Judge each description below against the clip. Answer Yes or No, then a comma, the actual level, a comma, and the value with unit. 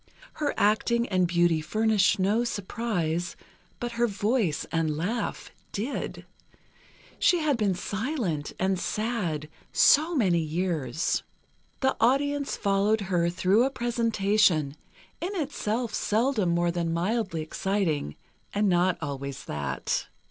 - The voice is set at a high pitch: Yes, high, 200 Hz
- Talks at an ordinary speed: No, slow, 120 wpm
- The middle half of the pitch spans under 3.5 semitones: No, wide, 5.5 semitones